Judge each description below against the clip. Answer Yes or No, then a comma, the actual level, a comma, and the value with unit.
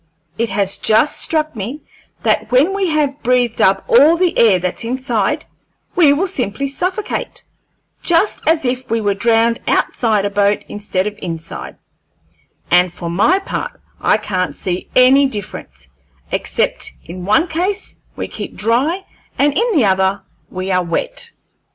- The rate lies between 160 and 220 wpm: No, average, 150 wpm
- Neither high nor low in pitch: No, high, 235 Hz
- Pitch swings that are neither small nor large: No, wide, 7.7 semitones